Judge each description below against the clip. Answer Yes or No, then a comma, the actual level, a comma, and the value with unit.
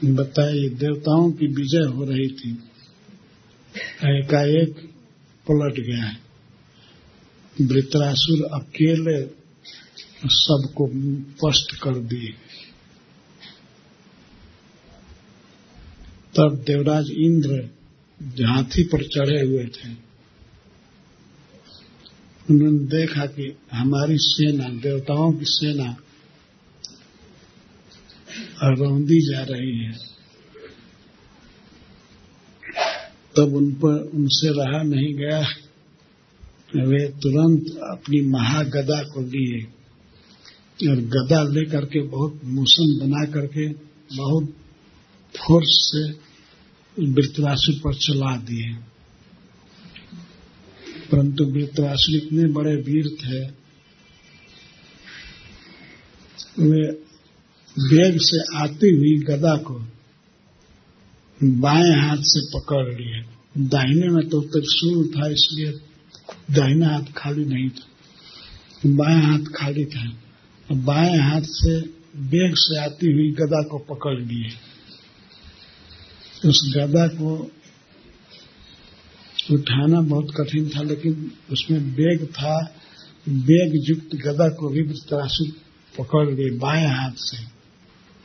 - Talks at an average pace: No, slow, 90 wpm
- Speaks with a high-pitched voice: No, medium, 145 Hz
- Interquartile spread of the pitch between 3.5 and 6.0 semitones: No, narrow, 2.5 semitones